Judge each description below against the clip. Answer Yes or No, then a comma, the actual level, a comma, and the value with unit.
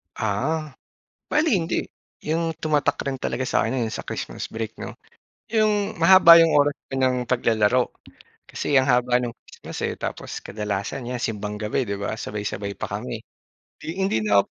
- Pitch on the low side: Yes, low, 130 Hz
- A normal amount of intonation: No, wide, 6.5 semitones